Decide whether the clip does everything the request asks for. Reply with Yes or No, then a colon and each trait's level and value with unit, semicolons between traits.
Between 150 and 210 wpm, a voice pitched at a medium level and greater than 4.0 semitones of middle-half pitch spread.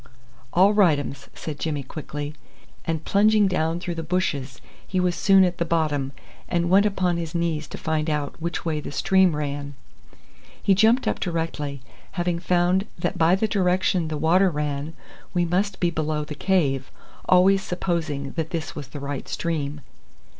No: average, 170 wpm; medium, 165 Hz; average, 3.5 semitones